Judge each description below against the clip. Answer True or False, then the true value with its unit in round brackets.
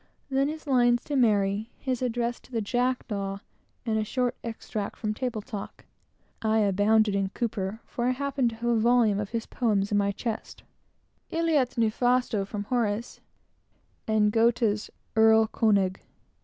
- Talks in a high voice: True (225 Hz)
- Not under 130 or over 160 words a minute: True (155 wpm)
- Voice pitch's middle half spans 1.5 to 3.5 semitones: True (2.9 semitones)